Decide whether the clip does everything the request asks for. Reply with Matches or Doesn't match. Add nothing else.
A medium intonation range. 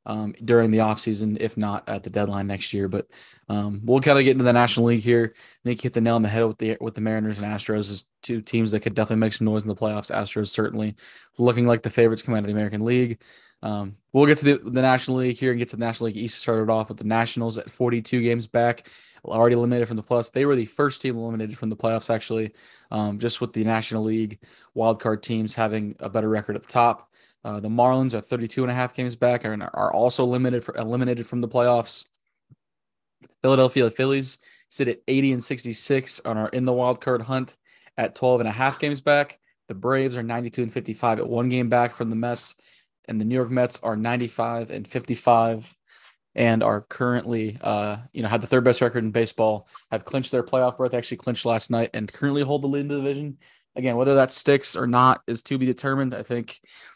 Doesn't match